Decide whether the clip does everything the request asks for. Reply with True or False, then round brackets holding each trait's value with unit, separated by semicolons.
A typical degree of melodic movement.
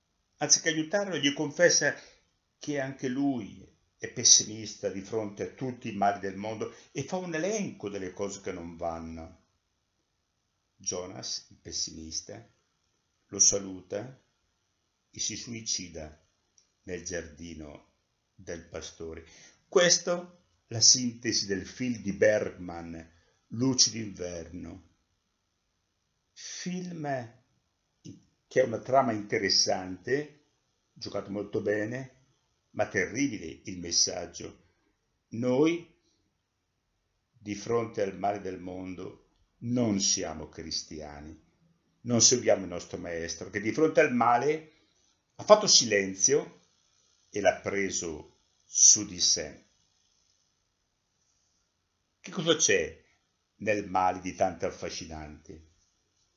False (5.8 semitones)